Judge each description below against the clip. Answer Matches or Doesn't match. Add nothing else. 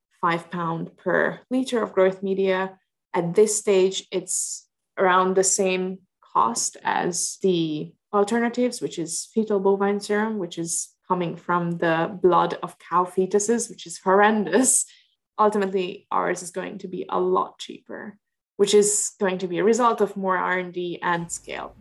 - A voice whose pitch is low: Doesn't match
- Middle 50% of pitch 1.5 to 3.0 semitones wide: Matches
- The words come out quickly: Doesn't match